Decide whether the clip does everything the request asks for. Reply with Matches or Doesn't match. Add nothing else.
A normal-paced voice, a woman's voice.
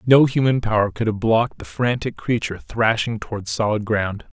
Doesn't match